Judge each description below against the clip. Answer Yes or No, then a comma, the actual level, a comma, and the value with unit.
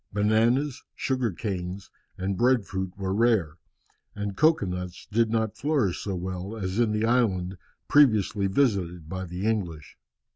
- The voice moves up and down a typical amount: Yes, average, 3.8 semitones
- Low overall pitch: Yes, low, 100 Hz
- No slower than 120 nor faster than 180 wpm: Yes, average, 145 wpm